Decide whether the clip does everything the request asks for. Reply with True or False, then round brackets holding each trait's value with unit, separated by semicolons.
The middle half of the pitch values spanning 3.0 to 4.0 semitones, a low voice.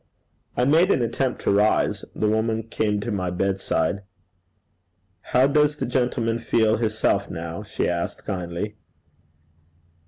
True (3.7 semitones; 110 Hz)